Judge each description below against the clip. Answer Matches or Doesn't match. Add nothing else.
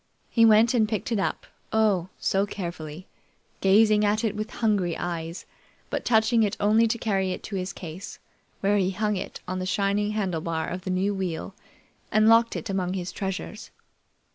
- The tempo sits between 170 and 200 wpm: Matches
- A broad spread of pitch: Doesn't match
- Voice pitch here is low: Doesn't match